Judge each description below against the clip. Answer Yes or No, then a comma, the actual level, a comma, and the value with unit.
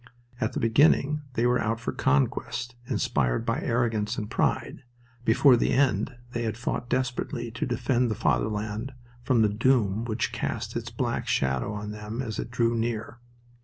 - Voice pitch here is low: Yes, low, 115 Hz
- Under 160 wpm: No, average, 165 wpm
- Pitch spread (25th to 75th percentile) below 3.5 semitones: Yes, narrow, 2.4 semitones